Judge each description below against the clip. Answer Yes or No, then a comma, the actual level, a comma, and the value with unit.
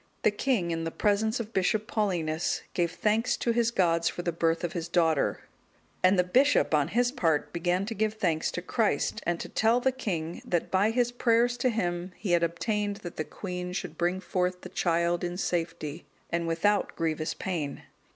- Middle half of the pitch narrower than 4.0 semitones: No, average, 4.3 semitones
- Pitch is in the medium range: Yes, medium, 180 Hz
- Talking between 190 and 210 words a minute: Yes, average, 195 wpm